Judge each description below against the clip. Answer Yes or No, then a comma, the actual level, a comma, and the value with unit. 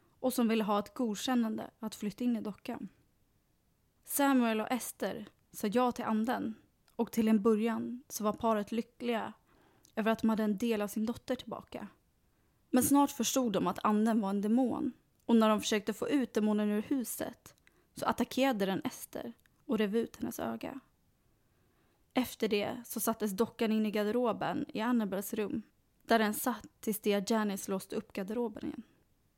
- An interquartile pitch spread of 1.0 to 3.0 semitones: Yes, narrow, 2.4 semitones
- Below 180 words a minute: Yes, average, 170 wpm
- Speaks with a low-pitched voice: No, high, 225 Hz